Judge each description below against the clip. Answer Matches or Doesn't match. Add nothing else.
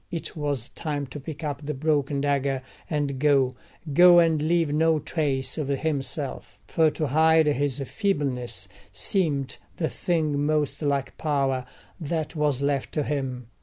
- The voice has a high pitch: Doesn't match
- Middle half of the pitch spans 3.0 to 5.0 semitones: Doesn't match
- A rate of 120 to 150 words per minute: Matches